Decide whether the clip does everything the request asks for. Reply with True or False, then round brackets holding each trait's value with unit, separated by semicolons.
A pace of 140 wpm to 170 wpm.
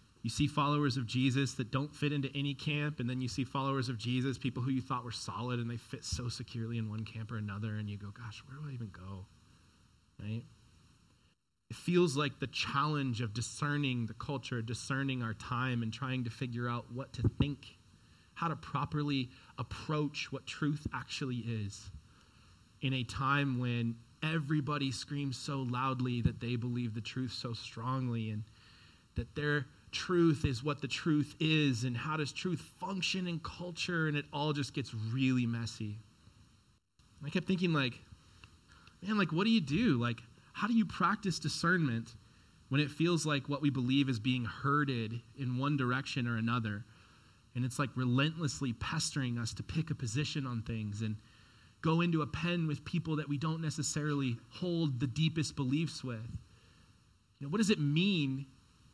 False (180 wpm)